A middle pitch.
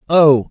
Yes: medium, 145 Hz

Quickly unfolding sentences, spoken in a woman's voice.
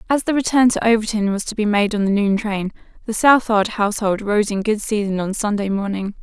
Yes: fast, 220 wpm; female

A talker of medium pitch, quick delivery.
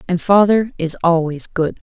No: medium, 180 Hz; average, 155 wpm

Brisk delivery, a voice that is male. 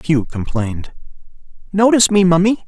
No: slow, 110 wpm; male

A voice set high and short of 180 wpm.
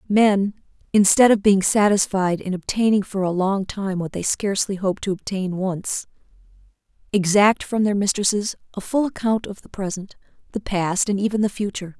Yes: high, 200 Hz; average, 170 wpm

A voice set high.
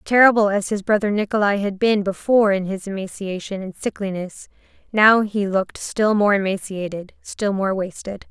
Yes: high, 200 Hz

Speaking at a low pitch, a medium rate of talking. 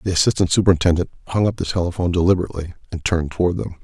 Yes: very low, 90 Hz; average, 190 wpm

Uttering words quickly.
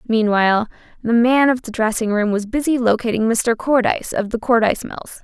No: average, 185 wpm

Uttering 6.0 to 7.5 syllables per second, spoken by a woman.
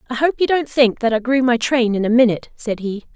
Yes: 6.1 syllables/s; female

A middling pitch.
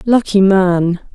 No: high, 195 Hz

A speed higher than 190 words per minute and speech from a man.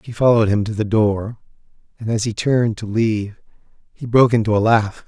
Yes: average, 200 wpm; male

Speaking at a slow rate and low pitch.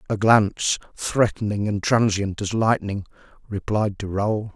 Yes: slow, 130 wpm; low, 105 Hz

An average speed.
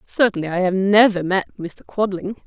Yes: average, 170 wpm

